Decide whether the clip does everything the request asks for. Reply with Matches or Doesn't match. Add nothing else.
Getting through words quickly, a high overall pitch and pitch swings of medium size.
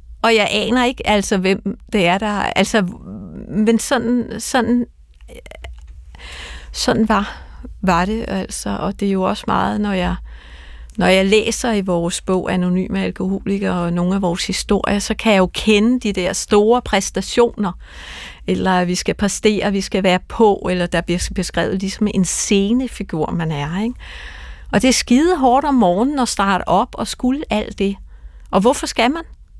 Doesn't match